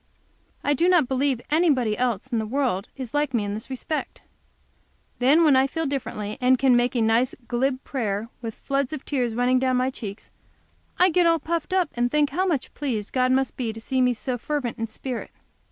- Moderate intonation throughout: Yes, average, 3.4 semitones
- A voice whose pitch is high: Yes, very high, 255 Hz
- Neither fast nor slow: No, fast, 210 wpm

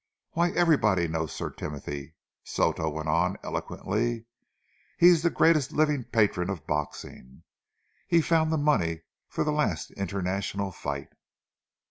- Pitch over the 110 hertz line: No, low, 100 Hz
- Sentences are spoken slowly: Yes, slow, 130 wpm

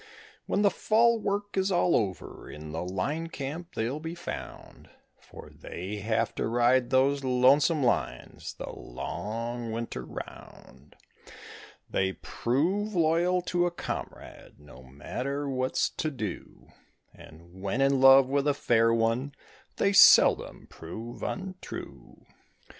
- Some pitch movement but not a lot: No, wide, 6.8 semitones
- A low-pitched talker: Yes, low, 130 Hz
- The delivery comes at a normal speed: No, slow, 130 wpm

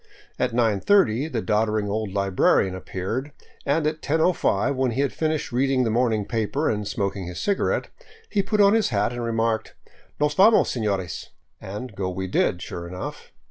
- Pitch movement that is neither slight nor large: No, wide, 6.0 semitones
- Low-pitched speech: Yes, low, 115 Hz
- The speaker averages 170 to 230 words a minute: Yes, average, 185 wpm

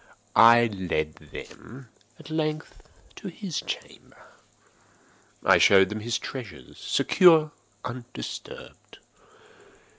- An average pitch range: No, wide, 7.3 semitones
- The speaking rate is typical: No, slow, 90 wpm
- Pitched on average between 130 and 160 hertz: No, low, 120 Hz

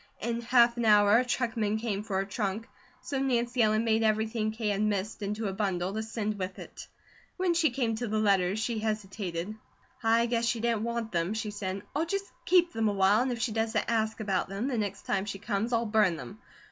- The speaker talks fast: Yes, fast, 220 wpm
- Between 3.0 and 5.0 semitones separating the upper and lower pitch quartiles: No, narrow, 2.5 semitones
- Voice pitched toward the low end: No, high, 220 Hz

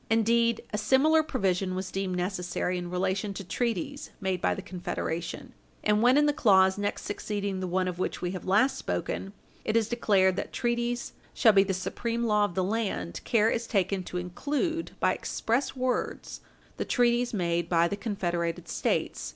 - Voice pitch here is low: No, high, 205 Hz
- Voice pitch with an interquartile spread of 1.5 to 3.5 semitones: No, average, 4.3 semitones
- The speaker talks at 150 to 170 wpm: No, average, 180 wpm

